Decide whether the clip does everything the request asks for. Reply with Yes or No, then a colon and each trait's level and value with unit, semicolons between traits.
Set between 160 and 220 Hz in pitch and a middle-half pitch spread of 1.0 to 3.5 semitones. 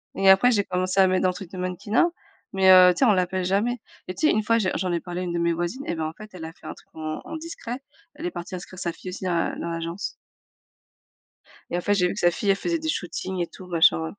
Yes: medium, 185 Hz; average, 3.1 semitones